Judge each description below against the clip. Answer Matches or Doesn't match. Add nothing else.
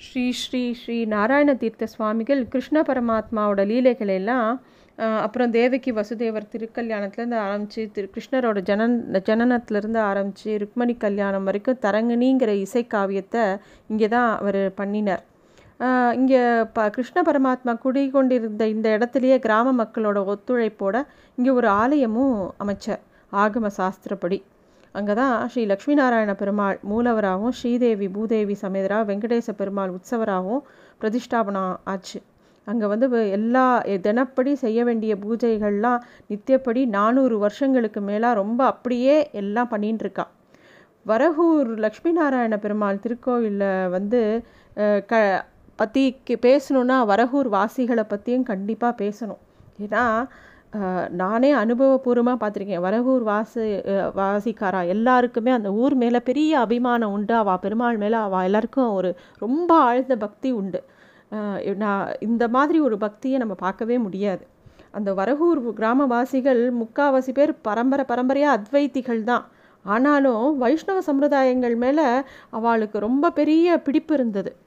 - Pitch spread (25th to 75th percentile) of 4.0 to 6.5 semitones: Doesn't match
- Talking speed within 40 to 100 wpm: Doesn't match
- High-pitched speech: Matches